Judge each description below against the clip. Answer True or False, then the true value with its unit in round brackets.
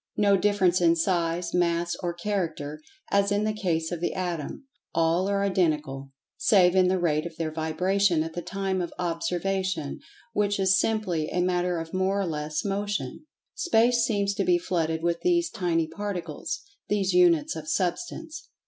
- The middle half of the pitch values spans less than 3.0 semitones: False (3.3 semitones)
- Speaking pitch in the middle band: True (180 Hz)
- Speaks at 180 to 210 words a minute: False (165 wpm)